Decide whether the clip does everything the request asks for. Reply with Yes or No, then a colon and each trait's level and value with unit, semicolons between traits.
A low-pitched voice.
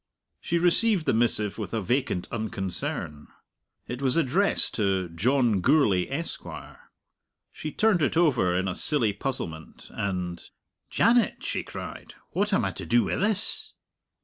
Yes: low, 120 Hz